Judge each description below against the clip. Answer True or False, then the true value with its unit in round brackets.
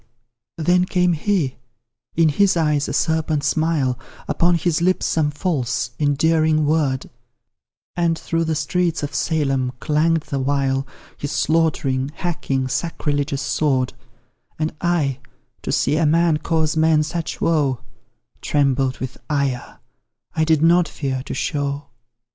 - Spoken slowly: True (130 wpm)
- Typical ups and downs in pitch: True (3.0 semitones)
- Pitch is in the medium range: True (150 Hz)